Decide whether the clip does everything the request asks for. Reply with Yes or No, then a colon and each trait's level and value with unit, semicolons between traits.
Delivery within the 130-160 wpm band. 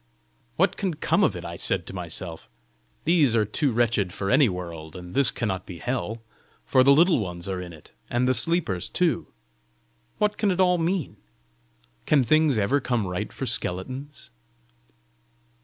No: average, 170 wpm